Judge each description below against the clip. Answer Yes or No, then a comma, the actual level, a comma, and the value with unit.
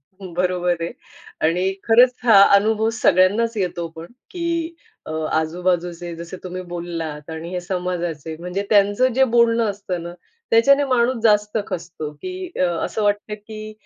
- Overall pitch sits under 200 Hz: Yes, high, 190 Hz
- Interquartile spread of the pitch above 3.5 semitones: Yes, average, 4.6 semitones